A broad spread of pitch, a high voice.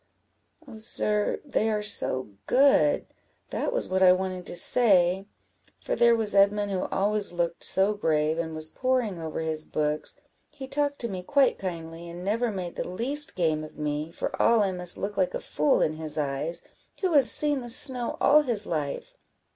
Yes: wide, 6.2 semitones; high, 195 Hz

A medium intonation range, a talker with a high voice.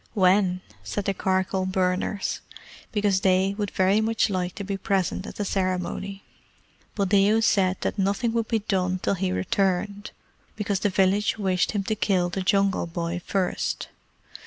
No: narrow, 1.7 semitones; high, 195 Hz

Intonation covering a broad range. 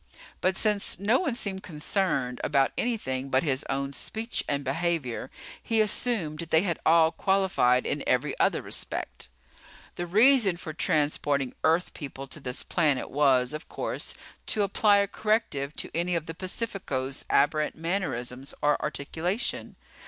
Yes: wide, 6.1 semitones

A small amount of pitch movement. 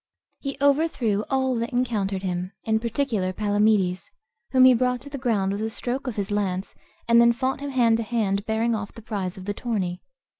No: average, 3.9 semitones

